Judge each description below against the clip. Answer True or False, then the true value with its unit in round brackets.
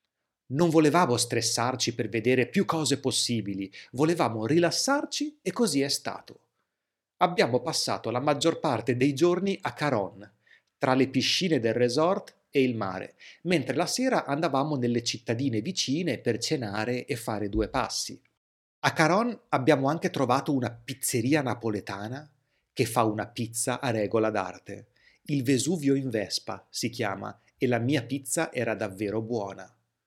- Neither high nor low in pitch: False (130 Hz)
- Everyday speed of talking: True (145 wpm)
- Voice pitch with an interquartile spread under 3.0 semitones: False (5.1 semitones)